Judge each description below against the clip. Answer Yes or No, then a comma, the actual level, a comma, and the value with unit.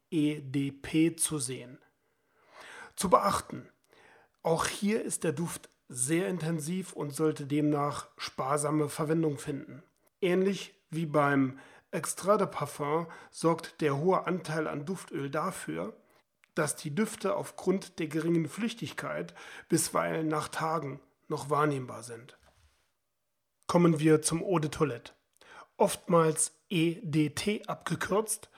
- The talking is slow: Yes, slow, 110 wpm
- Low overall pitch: No, medium, 160 Hz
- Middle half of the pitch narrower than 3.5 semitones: Yes, average, 2.8 semitones